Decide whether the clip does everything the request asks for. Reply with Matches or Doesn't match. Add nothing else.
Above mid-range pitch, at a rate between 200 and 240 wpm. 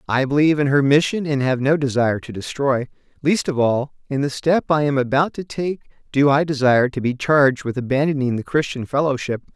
Doesn't match